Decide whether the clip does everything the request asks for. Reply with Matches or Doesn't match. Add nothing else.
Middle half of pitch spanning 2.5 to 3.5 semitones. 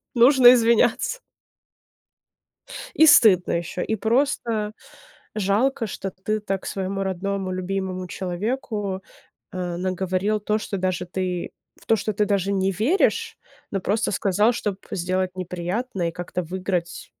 Matches